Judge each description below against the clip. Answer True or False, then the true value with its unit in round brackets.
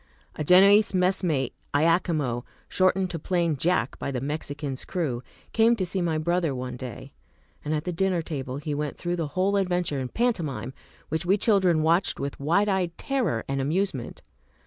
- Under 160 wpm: False (170 wpm)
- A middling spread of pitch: True (4.8 semitones)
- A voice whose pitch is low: False (165 Hz)